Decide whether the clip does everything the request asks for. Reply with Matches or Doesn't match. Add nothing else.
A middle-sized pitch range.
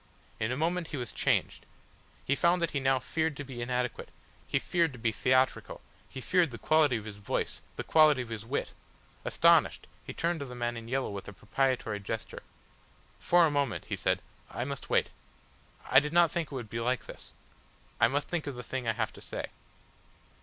Matches